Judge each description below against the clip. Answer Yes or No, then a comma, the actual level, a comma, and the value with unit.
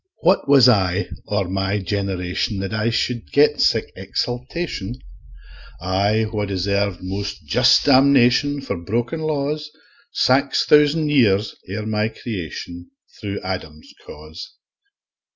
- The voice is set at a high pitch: No, low, 105 Hz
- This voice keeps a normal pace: No, slow, 115 wpm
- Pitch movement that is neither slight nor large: No, wide, 5.8 semitones